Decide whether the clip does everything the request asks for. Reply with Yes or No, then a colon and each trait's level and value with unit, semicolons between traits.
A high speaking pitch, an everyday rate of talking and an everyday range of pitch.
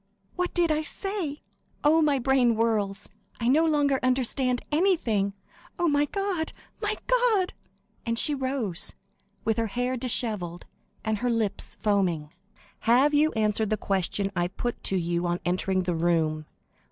No: high, 235 Hz; average, 150 wpm; wide, 7.1 semitones